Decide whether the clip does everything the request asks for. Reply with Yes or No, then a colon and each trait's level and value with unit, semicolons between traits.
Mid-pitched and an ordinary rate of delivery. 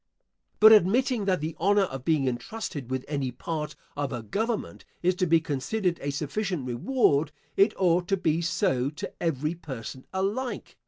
Yes: medium, 165 Hz; average, 165 wpm